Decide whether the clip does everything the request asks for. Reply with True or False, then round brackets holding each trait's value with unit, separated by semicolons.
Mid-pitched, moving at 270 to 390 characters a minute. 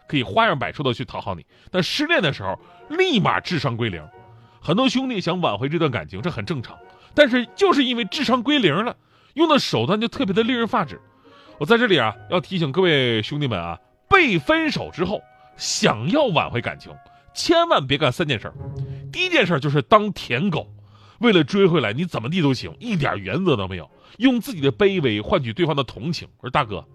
True (165 Hz; 310 characters per minute)